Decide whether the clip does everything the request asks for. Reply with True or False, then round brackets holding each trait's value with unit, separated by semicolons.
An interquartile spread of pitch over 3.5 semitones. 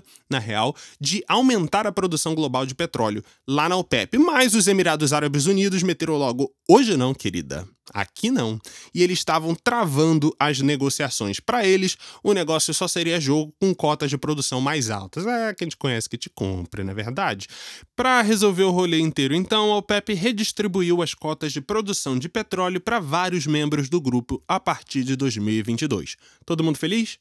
True (5.6 semitones)